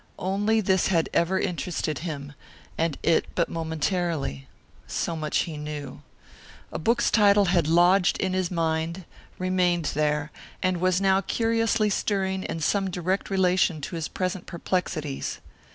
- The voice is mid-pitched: Yes, medium, 180 Hz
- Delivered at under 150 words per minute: Yes, average, 140 wpm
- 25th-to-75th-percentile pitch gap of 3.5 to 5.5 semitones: No, average, 3.0 semitones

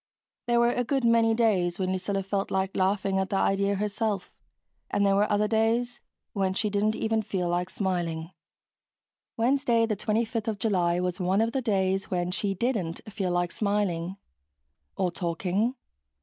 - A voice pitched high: Yes, high, 200 Hz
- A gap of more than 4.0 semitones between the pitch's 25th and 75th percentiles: No, average, 3.2 semitones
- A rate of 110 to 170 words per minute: Yes, average, 165 wpm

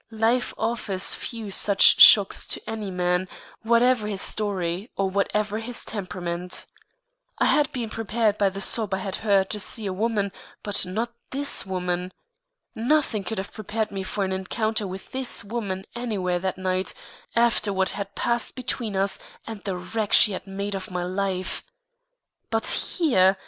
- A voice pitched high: Yes, high, 200 Hz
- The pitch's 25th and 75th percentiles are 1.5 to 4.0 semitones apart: Yes, average, 2.9 semitones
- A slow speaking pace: No, average, 165 wpm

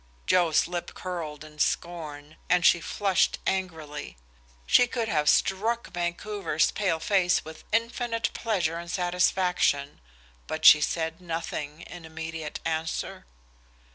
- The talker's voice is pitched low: No, medium, 170 Hz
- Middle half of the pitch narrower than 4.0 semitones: Yes, average, 3.0 semitones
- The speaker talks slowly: Yes, slow, 120 wpm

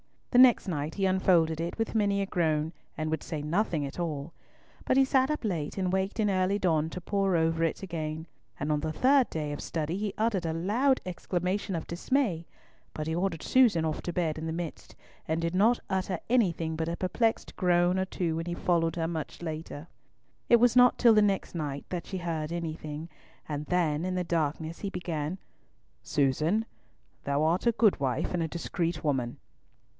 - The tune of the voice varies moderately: Yes, average, 3.6 semitones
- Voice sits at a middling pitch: Yes, medium, 170 Hz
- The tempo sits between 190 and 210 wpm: Yes, average, 200 wpm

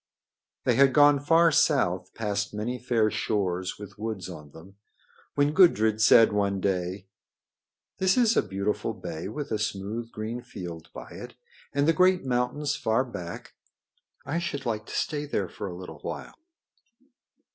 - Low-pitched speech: Yes, low, 110 Hz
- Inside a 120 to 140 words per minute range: No, average, 155 wpm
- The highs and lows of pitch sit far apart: Yes, wide, 6.4 semitones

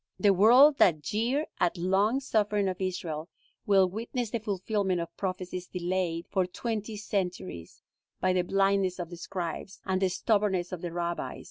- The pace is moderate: Yes, average, 165 wpm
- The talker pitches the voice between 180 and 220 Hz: Yes, high, 190 Hz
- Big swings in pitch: No, average, 2.7 semitones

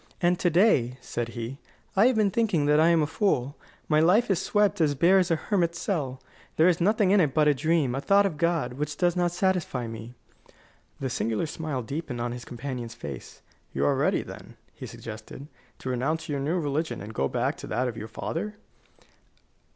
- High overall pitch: No, medium, 155 Hz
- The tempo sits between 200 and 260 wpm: Yes, fast, 205 wpm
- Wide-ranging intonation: Yes, wide, 5.8 semitones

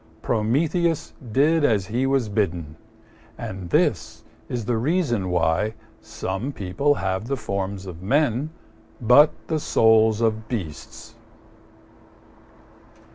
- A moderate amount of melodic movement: No, wide, 6.2 semitones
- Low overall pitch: Yes, low, 110 Hz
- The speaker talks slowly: Yes, slow, 110 wpm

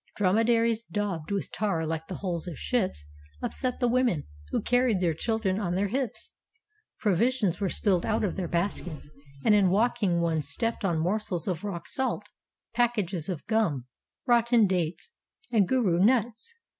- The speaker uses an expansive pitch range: No, average, 5.0 semitones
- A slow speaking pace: No, average, 165 wpm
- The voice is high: Yes, high, 200 Hz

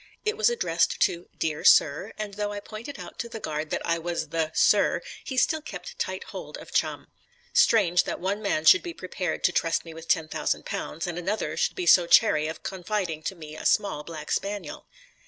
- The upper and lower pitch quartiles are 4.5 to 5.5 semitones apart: Yes, average, 4.8 semitones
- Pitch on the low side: No, medium, 180 Hz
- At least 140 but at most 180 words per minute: No, fast, 205 wpm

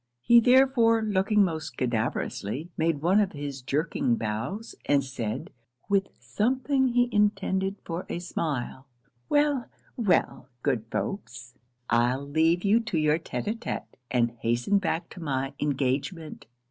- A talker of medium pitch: Yes, medium, 165 Hz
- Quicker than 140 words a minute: No, slow, 135 wpm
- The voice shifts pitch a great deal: Yes, wide, 7.9 semitones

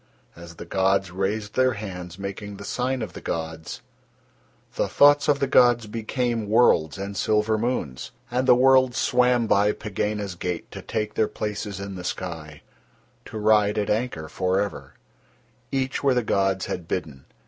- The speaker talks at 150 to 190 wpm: Yes, average, 165 wpm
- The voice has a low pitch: Yes, low, 105 Hz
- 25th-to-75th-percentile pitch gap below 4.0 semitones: No, average, 4.5 semitones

